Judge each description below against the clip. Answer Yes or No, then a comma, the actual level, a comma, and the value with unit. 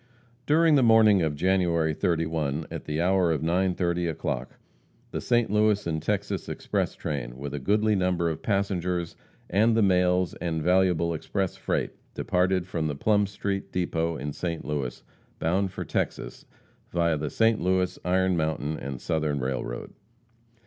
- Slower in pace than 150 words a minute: No, average, 155 wpm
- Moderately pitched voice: No, very low, 90 Hz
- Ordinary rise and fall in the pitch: Yes, average, 3.3 semitones